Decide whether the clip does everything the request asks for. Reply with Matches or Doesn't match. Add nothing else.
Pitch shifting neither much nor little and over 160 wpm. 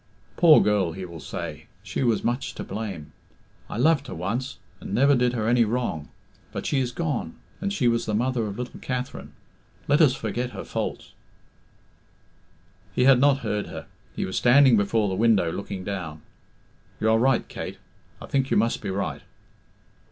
Matches